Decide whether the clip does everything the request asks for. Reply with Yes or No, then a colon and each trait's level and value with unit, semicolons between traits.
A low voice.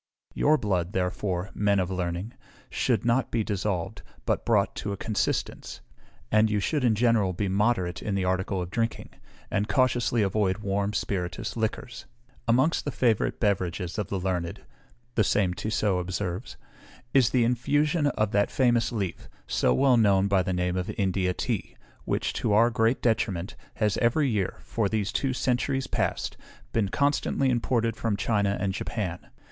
Yes: low, 105 Hz